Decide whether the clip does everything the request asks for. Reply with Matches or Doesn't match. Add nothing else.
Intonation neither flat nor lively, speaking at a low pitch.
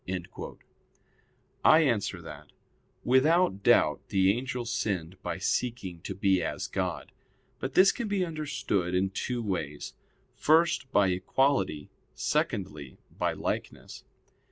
Doesn't match